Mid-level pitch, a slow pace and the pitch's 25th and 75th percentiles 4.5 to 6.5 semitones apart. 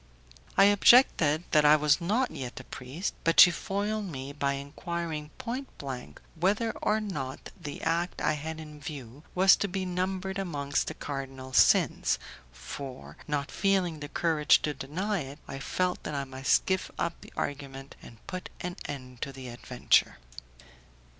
No: medium, 150 Hz; average, 165 wpm; average, 5.1 semitones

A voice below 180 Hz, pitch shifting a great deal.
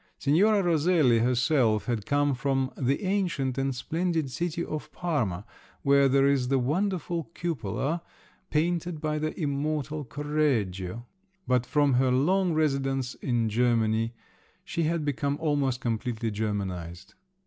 No: medium, 140 Hz; average, 4.3 semitones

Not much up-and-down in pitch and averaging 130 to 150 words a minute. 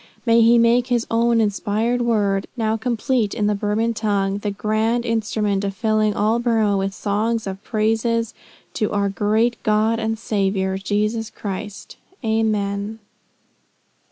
Yes: narrow, 2.0 semitones; average, 140 wpm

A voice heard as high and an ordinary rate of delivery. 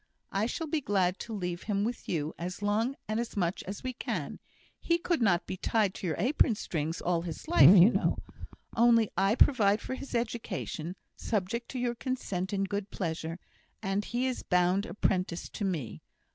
Yes: high, 200 Hz; average, 185 wpm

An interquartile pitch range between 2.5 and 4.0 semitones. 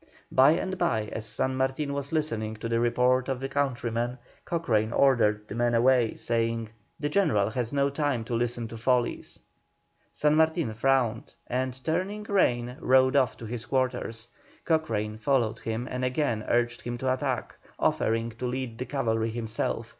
Yes: average, 3.0 semitones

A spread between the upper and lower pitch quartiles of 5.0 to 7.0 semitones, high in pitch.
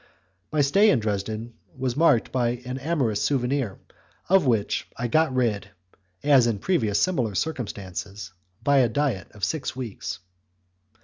No: average, 5.3 semitones; low, 125 Hz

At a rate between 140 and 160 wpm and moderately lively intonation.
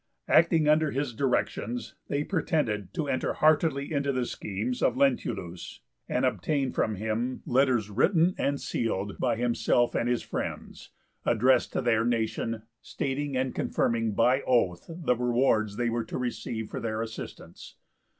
Yes: average, 150 wpm; average, 3.7 semitones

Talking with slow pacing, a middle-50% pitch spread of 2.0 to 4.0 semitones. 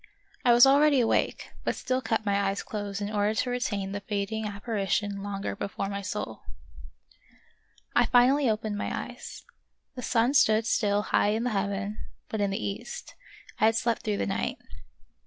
No: average, 175 wpm; average, 2.9 semitones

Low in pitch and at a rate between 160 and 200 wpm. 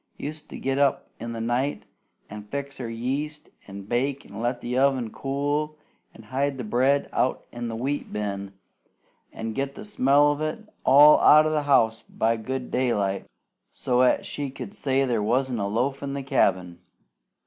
Yes: low, 130 Hz; average, 180 wpm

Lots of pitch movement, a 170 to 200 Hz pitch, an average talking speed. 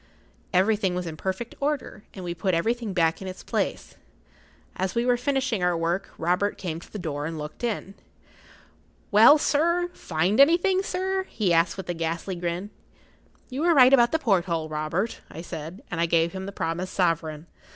Yes: wide, 6.2 semitones; medium, 185 Hz; average, 180 wpm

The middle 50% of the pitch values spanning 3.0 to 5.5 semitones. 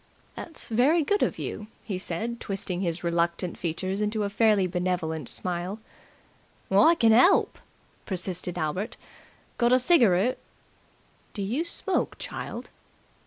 Yes: average, 4.9 semitones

